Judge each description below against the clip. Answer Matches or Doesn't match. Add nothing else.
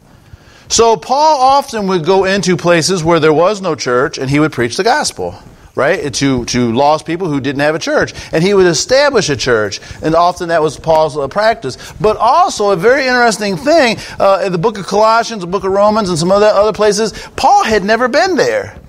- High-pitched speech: Matches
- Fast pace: Matches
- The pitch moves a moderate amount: Doesn't match